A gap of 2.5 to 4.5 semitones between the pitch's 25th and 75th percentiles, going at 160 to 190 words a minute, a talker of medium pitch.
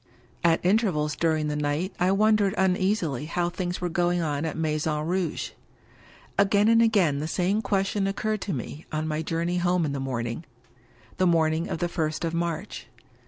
Yes: average, 3.6 semitones; average, 185 wpm; medium, 170 Hz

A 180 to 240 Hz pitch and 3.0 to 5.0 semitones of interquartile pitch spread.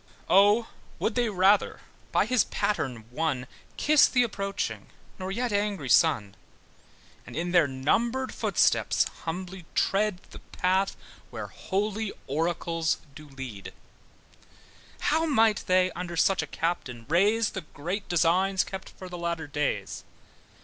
Yes: medium, 185 Hz; average, 4.5 semitones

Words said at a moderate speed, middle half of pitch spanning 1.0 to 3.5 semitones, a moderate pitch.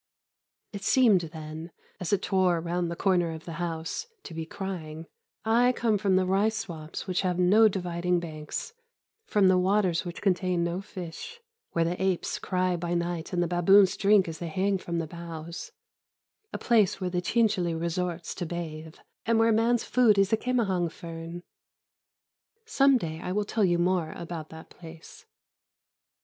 Yes: average, 170 wpm; average, 3.0 semitones; medium, 180 Hz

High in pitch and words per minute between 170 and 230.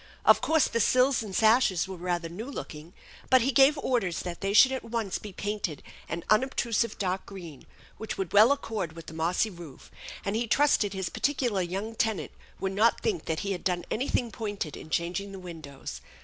Yes: high, 200 Hz; average, 195 wpm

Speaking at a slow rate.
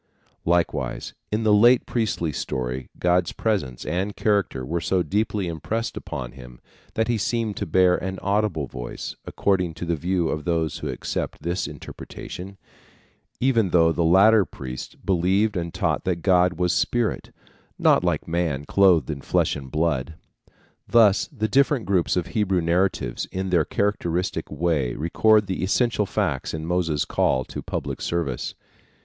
No: average, 155 wpm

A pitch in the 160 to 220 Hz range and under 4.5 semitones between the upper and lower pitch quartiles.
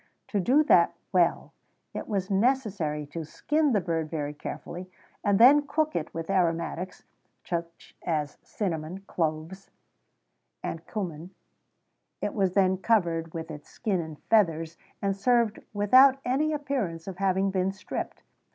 No: high, 190 Hz; average, 4.8 semitones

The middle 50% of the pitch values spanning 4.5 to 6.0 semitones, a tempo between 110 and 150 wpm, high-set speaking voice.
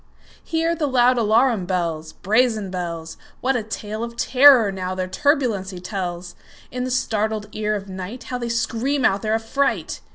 Yes: average, 4.9 semitones; average, 140 wpm; high, 220 Hz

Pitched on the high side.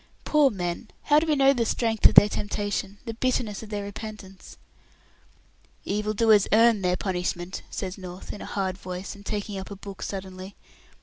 Yes: high, 205 Hz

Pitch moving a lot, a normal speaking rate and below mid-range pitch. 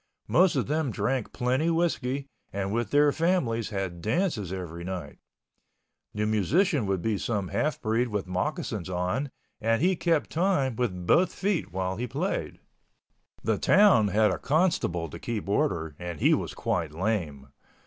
Yes: wide, 7.9 semitones; average, 160 wpm; low, 110 Hz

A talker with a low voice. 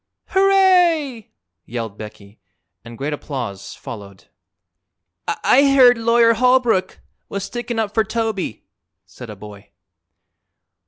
No: high, 215 Hz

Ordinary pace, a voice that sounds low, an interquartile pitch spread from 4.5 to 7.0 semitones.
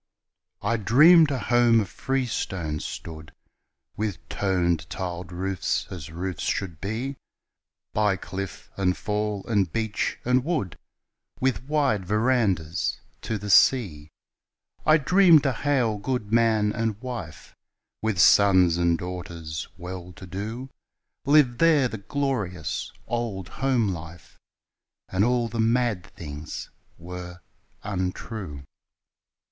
No: slow, 115 wpm; low, 105 Hz; average, 5.3 semitones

